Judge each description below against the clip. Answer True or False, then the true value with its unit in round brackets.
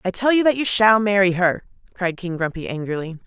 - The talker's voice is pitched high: True (195 Hz)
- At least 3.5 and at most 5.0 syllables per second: False (5.7 syllables/s)